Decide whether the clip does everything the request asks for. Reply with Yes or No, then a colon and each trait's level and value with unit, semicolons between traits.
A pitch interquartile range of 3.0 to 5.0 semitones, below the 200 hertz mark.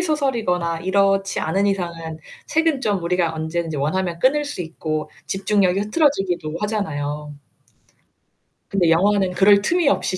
Yes: average, 3.9 semitones; high, 190 Hz